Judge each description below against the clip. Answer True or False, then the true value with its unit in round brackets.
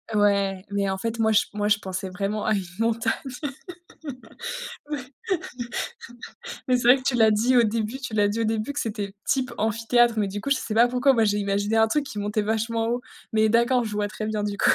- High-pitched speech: True (220 Hz)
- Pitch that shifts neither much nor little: False (2.2 semitones)